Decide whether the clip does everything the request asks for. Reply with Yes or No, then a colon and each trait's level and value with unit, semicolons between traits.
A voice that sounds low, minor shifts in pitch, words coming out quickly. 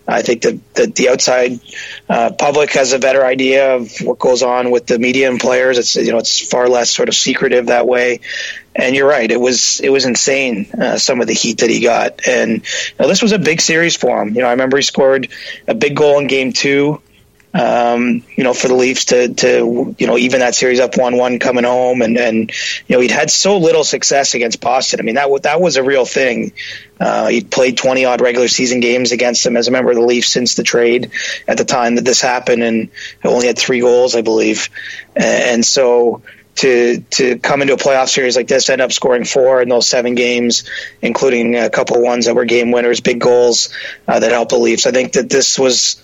Yes: low, 125 Hz; narrow, 1.6 semitones; fast, 235 wpm